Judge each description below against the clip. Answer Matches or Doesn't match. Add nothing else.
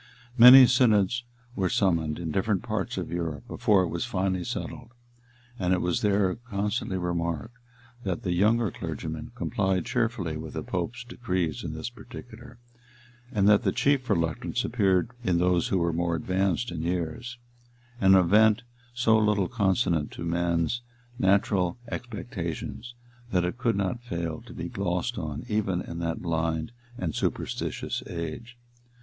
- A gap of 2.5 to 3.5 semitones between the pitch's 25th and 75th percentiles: Doesn't match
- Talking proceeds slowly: Doesn't match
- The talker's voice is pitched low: Matches